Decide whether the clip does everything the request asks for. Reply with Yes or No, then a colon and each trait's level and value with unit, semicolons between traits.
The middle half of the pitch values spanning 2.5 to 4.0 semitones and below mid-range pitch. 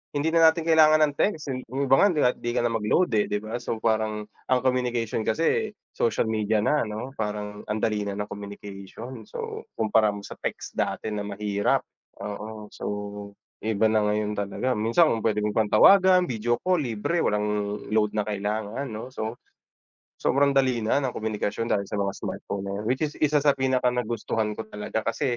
Yes: average, 3.6 semitones; low, 110 Hz